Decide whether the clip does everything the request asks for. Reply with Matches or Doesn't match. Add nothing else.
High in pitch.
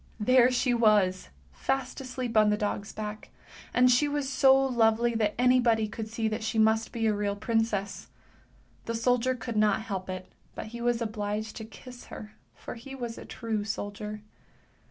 Matches